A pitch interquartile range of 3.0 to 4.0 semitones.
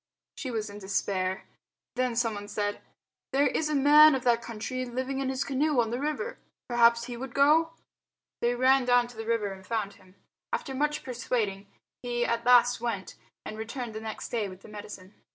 Yes: average, 3.5 semitones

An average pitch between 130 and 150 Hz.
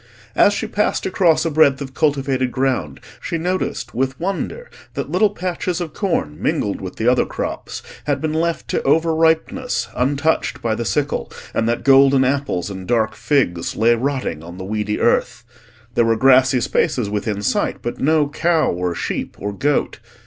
Yes: low, 135 Hz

